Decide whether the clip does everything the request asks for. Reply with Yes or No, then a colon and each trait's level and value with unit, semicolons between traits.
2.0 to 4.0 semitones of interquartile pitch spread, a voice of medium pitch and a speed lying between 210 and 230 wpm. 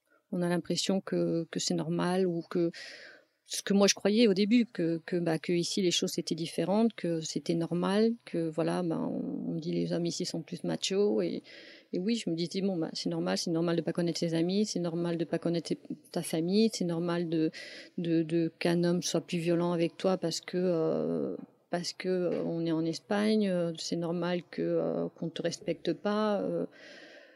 Yes: average, 2.8 semitones; medium, 175 Hz; average, 215 wpm